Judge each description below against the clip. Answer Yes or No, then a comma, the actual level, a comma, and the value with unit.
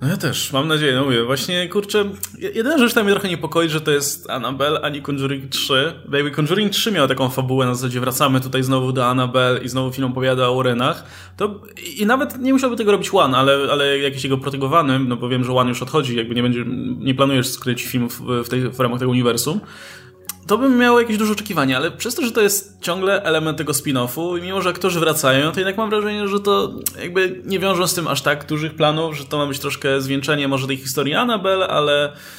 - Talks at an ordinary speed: No, fast, 225 wpm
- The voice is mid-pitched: Yes, medium, 145 Hz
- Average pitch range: No, wide, 6.4 semitones